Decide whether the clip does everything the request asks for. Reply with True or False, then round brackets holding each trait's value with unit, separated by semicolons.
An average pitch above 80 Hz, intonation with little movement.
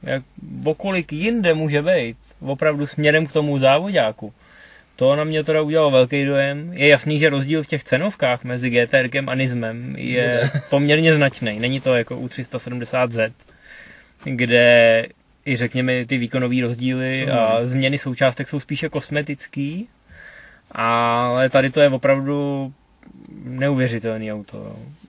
False (135 Hz; 3.2 semitones)